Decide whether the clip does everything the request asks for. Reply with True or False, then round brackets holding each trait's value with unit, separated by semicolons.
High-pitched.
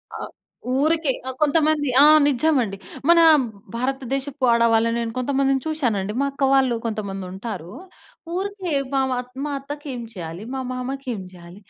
True (260 Hz)